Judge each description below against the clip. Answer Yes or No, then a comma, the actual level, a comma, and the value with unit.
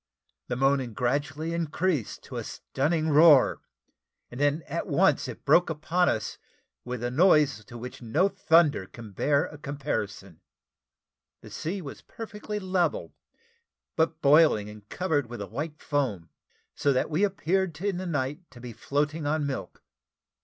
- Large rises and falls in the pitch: No, average, 4.8 semitones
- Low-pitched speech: No, medium, 145 Hz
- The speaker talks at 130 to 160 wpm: Yes, average, 155 wpm